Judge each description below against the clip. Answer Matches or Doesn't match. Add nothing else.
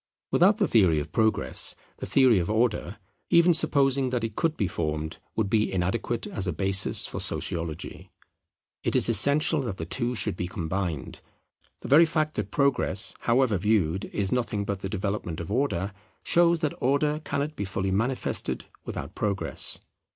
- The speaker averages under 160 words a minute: Doesn't match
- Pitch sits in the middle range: Doesn't match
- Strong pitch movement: Matches